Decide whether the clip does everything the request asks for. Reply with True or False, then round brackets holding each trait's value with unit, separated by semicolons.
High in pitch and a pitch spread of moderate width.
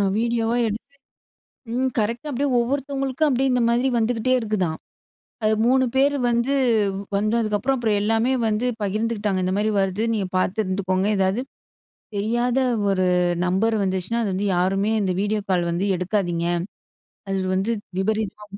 True (215 Hz; 3.7 semitones)